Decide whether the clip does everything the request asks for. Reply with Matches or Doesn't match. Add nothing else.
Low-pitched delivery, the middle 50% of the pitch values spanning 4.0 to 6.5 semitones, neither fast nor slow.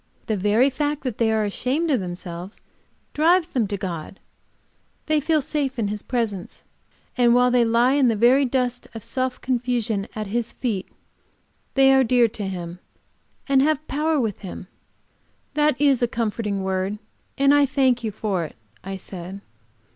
Doesn't match